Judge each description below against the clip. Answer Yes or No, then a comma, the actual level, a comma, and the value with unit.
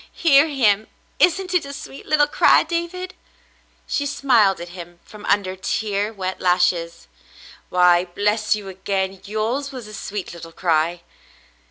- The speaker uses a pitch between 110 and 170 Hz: No, high, 205 Hz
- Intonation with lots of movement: Yes, wide, 7.3 semitones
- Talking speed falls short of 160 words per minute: Yes, average, 150 wpm